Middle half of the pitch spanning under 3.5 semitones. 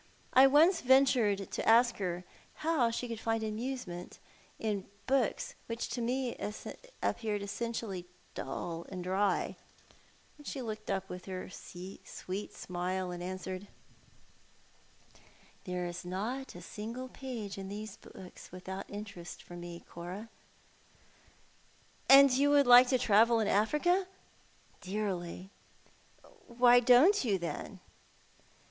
No: average, 5.2 semitones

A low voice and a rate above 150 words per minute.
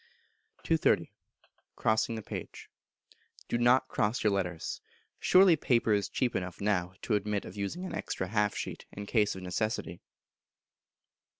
No: low, 105 Hz; average, 140 wpm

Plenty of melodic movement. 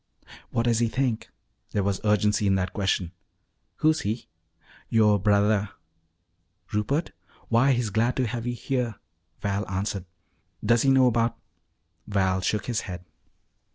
No: average, 3.1 semitones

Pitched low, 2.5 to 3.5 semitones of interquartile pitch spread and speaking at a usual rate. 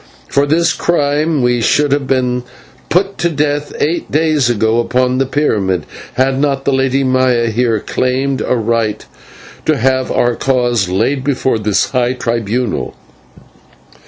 Yes: low, 130 Hz; average, 3.2 semitones; average, 145 wpm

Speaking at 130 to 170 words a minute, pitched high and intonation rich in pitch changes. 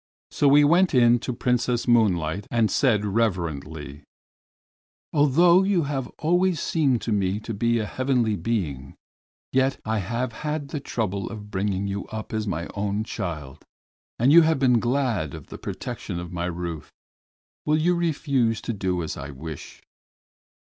No: average, 160 wpm; low, 115 Hz; wide, 6.5 semitones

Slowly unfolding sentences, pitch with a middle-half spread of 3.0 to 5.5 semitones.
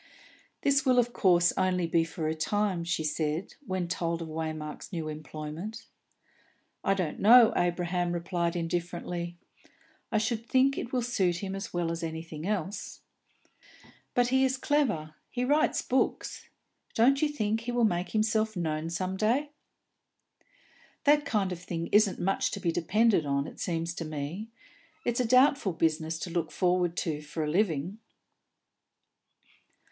No: average, 155 wpm; average, 5.2 semitones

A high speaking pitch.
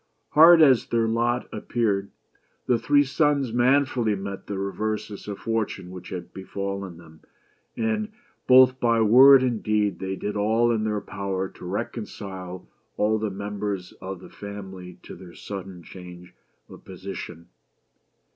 No: low, 105 Hz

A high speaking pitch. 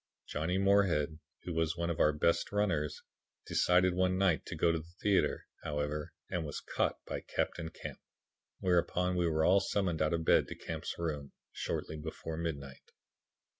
No: very low, 85 Hz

